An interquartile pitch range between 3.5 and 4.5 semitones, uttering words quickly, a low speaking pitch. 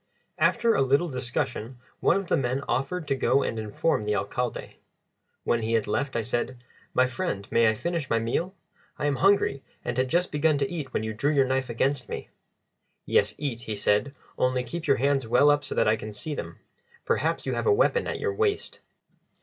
Yes: average, 4.1 semitones; fast, 210 wpm; low, 130 Hz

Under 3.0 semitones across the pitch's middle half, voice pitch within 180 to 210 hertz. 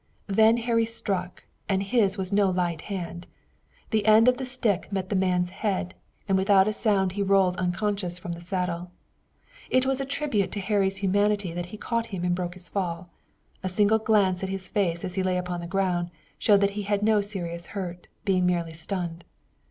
Yes: narrow, 2.6 semitones; high, 190 Hz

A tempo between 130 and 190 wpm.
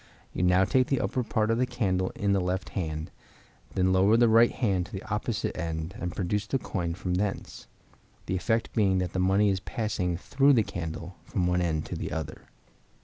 No: fast, 205 wpm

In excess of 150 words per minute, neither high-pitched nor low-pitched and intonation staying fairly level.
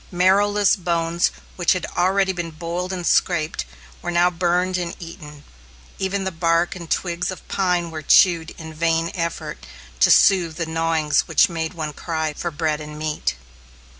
Yes: average, 165 wpm; medium, 170 Hz; narrow, 2.0 semitones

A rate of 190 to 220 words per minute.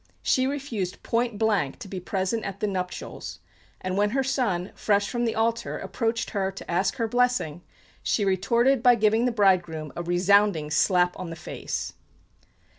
No: average, 170 wpm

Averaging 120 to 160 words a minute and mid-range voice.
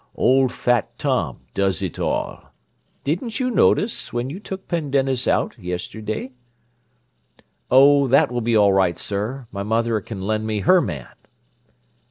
No: average, 145 wpm; low, 120 Hz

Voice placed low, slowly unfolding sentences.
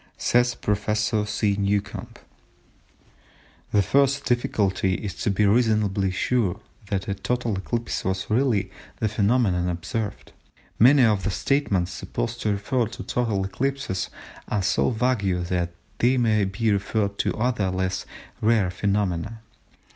Yes: low, 105 Hz; slow, 130 wpm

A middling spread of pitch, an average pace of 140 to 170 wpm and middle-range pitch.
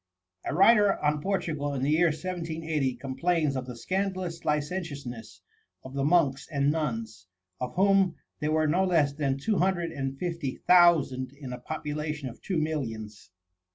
Yes: average, 4.3 semitones; average, 155 wpm; medium, 150 Hz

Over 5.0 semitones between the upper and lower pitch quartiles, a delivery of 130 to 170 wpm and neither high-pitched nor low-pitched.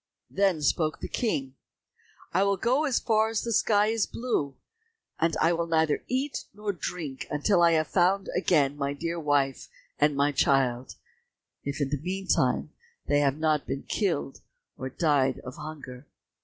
Yes: wide, 5.6 semitones; average, 160 wpm; medium, 160 Hz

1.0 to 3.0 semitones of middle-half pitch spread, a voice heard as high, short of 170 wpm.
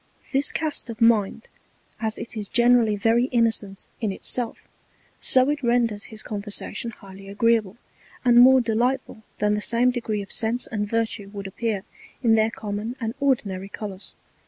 Yes: narrow, 2.6 semitones; high, 225 Hz; average, 160 wpm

